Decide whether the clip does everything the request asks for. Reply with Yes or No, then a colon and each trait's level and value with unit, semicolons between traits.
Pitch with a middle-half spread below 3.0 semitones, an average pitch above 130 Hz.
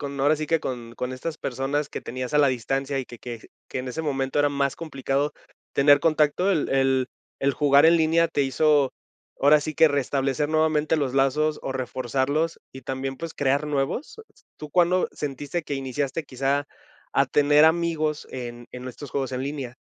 Yes: narrow, 2.5 semitones; medium, 140 Hz